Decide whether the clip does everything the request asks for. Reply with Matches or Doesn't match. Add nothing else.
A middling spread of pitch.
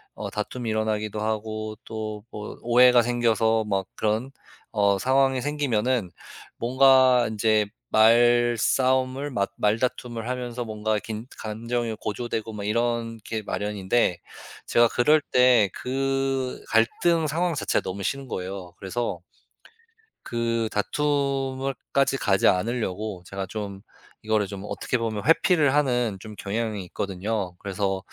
Matches